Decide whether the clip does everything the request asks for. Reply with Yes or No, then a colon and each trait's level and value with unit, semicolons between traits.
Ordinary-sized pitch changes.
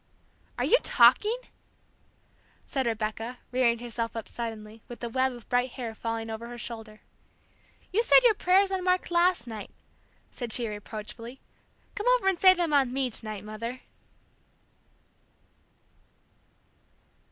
No: wide, 7.4 semitones